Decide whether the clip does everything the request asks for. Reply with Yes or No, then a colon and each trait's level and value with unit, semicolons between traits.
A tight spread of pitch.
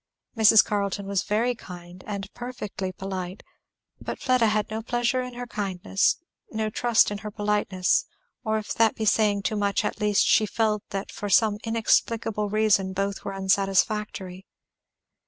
Yes: narrow, 2.1 semitones